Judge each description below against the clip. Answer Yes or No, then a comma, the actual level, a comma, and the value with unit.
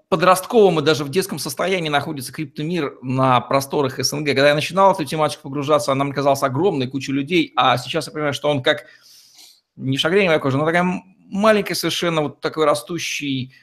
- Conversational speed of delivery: No, fast, 180 wpm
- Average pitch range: Yes, average, 3.7 semitones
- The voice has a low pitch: No, medium, 150 Hz